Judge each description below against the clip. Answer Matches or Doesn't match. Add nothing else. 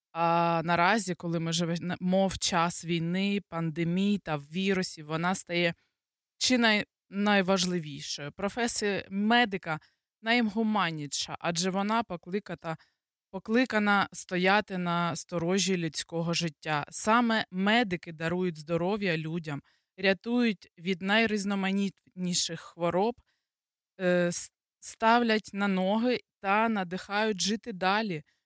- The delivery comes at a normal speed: Doesn't match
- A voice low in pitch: Doesn't match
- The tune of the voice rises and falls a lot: Doesn't match